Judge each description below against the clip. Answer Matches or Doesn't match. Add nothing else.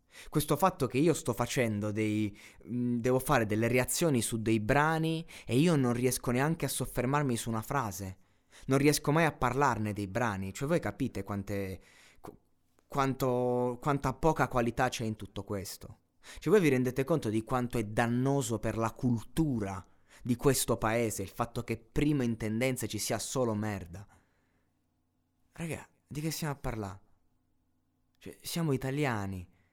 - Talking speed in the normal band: Matches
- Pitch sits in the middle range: Doesn't match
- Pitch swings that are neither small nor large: Matches